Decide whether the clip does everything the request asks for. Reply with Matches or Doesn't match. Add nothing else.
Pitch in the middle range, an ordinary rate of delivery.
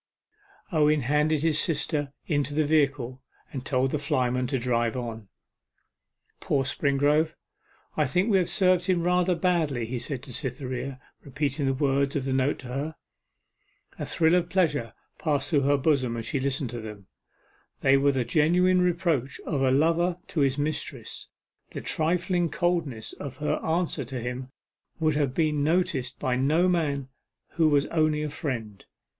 Matches